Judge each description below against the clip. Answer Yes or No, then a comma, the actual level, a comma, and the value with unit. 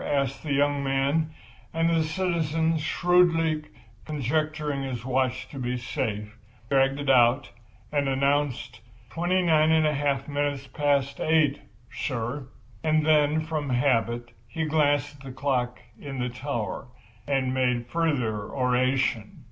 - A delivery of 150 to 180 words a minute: No, slow, 135 wpm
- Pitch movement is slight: No, average, 3.3 semitones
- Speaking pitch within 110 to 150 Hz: Yes, medium, 140 Hz